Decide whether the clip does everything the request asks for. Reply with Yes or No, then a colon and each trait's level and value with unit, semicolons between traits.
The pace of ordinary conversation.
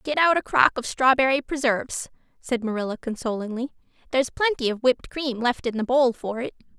Yes: average, 185 wpm